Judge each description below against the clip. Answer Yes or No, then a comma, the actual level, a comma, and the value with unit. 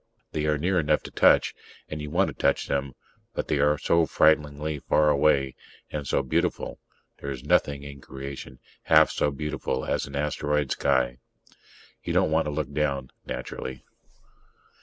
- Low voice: Yes, very low, 75 Hz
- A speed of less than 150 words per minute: No, average, 160 wpm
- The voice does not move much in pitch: Yes, narrow, 1.8 semitones